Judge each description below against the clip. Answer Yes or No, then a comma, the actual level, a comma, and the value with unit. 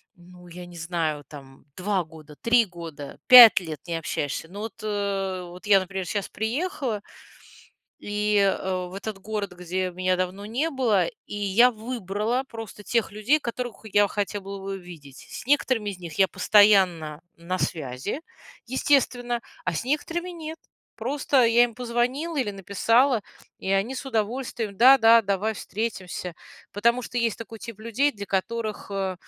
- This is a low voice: No, high, 205 Hz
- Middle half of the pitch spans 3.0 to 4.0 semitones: No, average, 4.4 semitones